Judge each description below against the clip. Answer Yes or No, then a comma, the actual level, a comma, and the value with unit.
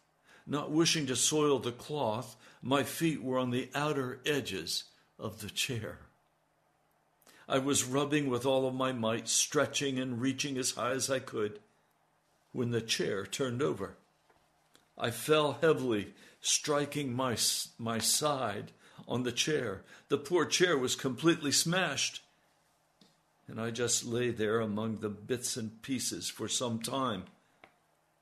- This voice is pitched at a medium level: No, low, 130 Hz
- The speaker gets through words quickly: No, average, 140 wpm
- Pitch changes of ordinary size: Yes, average, 3.2 semitones